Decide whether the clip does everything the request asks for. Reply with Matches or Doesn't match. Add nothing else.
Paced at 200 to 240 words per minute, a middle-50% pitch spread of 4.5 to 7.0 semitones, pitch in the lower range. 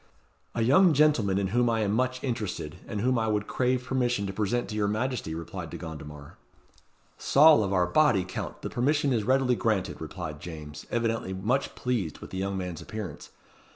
Doesn't match